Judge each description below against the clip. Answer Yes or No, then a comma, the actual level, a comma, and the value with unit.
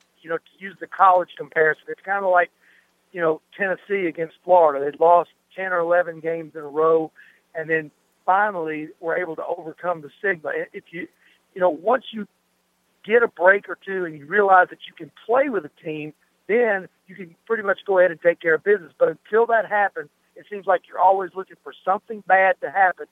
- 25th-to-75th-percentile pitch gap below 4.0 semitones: Yes, average, 3.3 semitones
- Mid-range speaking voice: Yes, medium, 180 Hz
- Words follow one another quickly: Yes, fast, 215 wpm